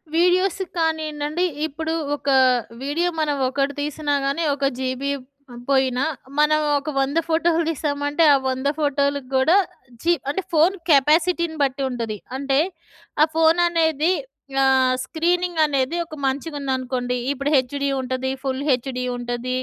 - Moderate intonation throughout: Yes, average, 3.3 semitones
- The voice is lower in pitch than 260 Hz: No, very high, 285 Hz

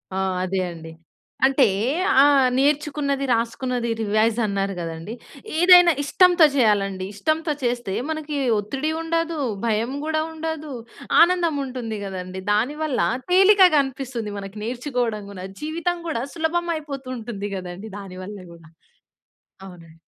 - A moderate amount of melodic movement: No, wide, 7.4 semitones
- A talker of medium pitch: No, very high, 250 Hz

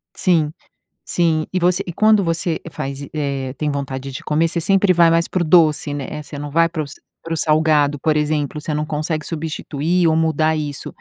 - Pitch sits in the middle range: Yes, medium, 155 Hz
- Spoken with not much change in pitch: Yes, narrow, 2.2 semitones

